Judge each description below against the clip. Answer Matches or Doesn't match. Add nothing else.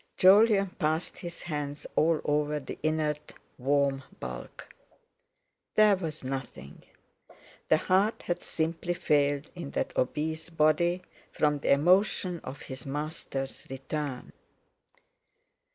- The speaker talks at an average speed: Doesn't match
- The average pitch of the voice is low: Doesn't match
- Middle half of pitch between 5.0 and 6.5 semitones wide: Doesn't match